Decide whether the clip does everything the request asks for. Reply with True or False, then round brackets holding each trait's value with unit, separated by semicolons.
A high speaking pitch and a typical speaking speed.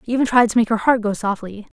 False (225 Hz; 305 wpm)